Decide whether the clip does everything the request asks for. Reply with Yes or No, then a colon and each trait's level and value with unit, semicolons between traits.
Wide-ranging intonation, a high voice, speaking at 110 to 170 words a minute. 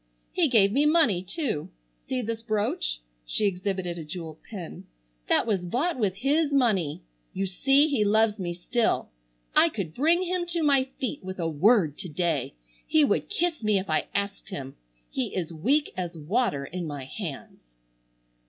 Yes: wide, 8.0 semitones; high, 200 Hz; average, 165 wpm